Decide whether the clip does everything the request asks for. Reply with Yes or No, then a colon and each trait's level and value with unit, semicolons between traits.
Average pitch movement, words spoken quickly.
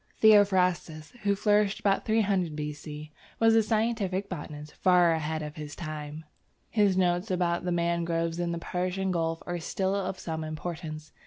No: average, 3.6 semitones; average, 155 wpm